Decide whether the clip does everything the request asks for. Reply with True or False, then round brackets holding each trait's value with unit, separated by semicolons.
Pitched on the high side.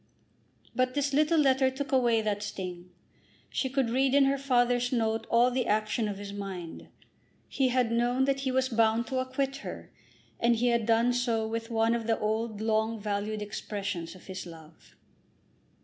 True (230 Hz)